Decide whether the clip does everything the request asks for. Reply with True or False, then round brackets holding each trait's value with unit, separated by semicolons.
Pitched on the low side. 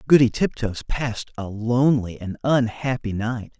True (120 Hz)